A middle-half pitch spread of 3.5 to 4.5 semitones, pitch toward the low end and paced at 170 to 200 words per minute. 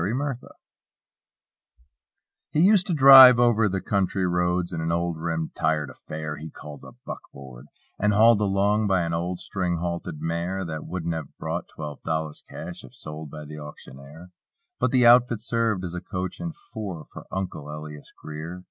No: average, 5.1 semitones; very low, 90 Hz; average, 175 wpm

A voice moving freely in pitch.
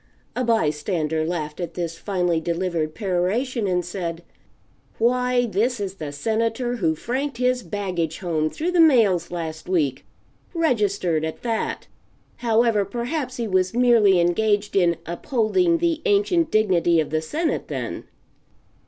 Yes: wide, 6.1 semitones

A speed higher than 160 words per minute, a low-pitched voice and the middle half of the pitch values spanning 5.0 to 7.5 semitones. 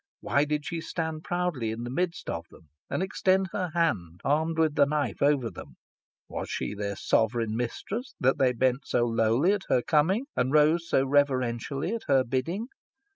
No: average, 180 wpm; medium, 145 Hz; wide, 5.6 semitones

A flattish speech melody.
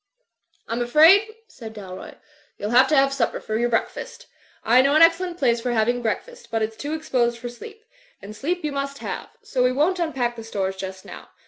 No: wide, 5.4 semitones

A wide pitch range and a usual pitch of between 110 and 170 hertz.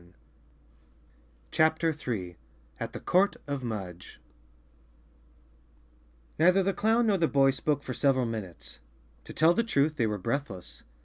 Yes: wide, 7.4 semitones; medium, 140 Hz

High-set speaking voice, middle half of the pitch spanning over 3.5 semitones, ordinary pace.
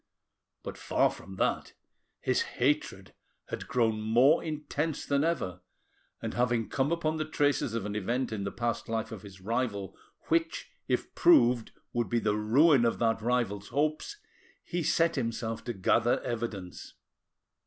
No: low, 120 Hz; average, 5.2 semitones; average, 155 wpm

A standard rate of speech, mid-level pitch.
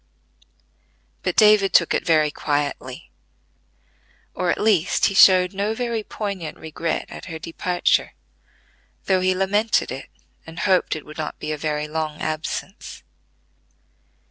No: slow, 130 wpm; medium, 175 Hz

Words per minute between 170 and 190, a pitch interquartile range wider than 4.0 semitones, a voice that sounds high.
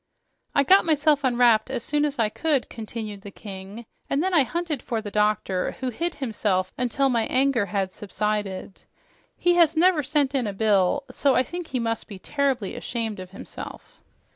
Yes: average, 185 wpm; wide, 5.4 semitones; high, 240 Hz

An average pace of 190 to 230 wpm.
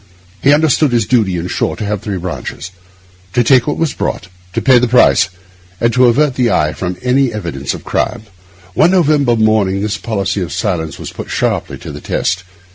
Yes: average, 200 wpm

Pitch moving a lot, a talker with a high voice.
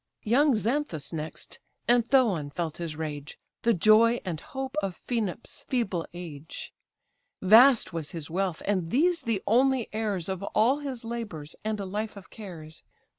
Yes: wide, 5.9 semitones; high, 205 Hz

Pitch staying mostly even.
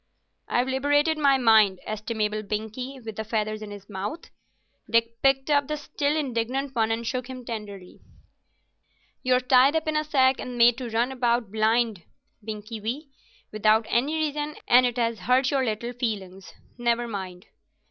No: average, 3.6 semitones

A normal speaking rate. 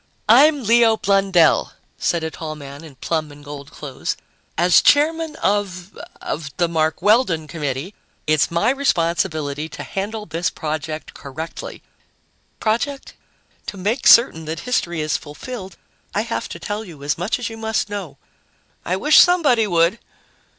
Yes: average, 150 wpm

